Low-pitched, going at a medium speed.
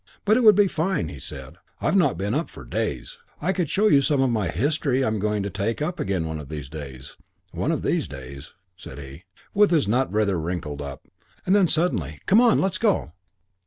No: low, 105 Hz; fast, 220 wpm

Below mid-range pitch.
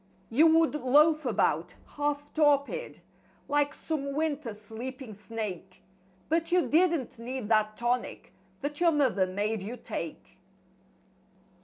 No: very high, 265 Hz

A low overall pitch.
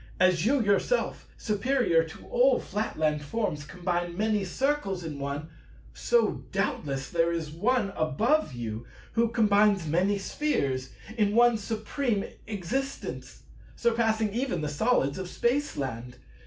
No: high, 200 Hz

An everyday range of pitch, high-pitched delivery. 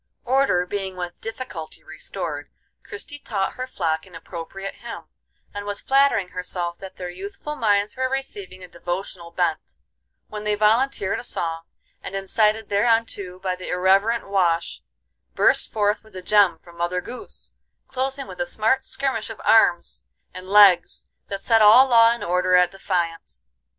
Yes: average, 4.1 semitones; high, 200 Hz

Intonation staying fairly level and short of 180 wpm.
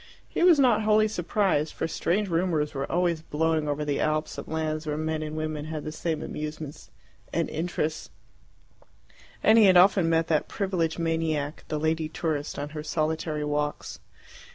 Yes: narrow, 2.2 semitones; average, 170 wpm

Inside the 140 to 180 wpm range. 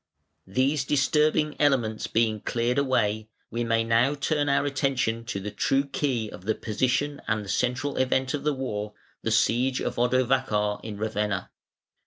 Yes: average, 165 wpm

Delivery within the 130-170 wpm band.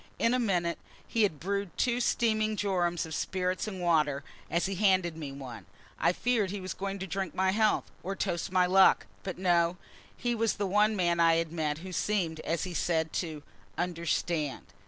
No: average, 195 wpm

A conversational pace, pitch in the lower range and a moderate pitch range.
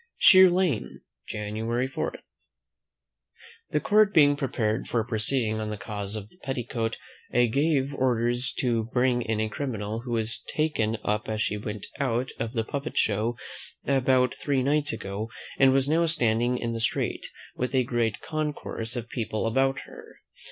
Yes: average, 160 wpm; low, 120 Hz; average, 3.7 semitones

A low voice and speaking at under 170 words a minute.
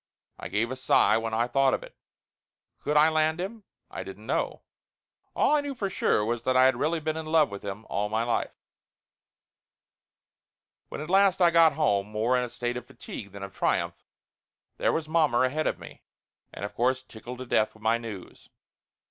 No: low, 130 Hz; average, 200 wpm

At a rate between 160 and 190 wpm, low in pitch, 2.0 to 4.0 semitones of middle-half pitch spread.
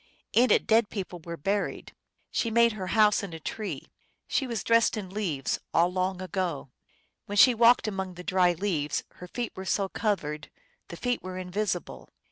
No: average, 180 wpm; high, 190 Hz; average, 3.3 semitones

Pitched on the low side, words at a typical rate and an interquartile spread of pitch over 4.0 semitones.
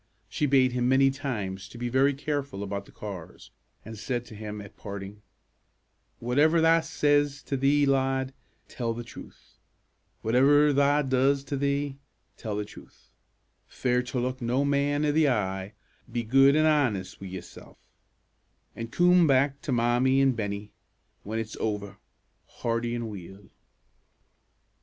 Yes: low, 125 Hz; average, 150 wpm; average, 4.6 semitones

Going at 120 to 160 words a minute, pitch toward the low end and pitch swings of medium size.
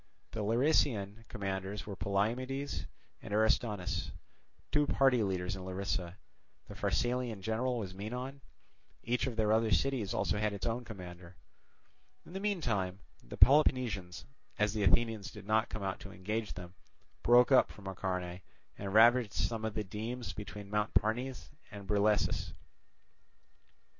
Yes: average, 145 wpm; low, 105 Hz; average, 3.7 semitones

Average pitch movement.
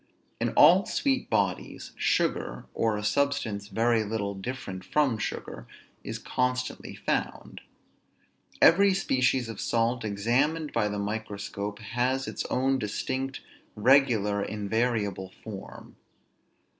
Yes: average, 4.4 semitones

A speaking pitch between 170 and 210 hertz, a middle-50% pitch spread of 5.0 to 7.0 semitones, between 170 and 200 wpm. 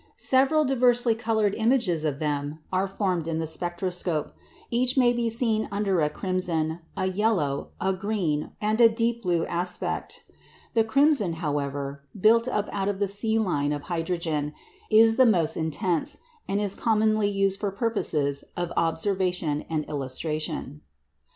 No: high, 190 Hz; wide, 5.6 semitones; average, 150 wpm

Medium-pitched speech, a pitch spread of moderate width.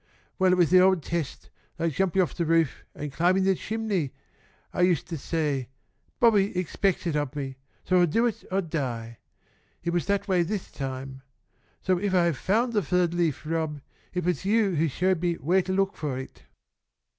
Yes: medium, 175 Hz; average, 3.8 semitones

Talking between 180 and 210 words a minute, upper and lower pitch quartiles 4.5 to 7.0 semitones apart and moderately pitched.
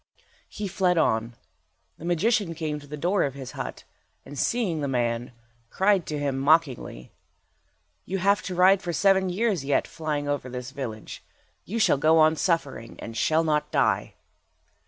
No: average, 165 wpm; average, 5.2 semitones; medium, 155 Hz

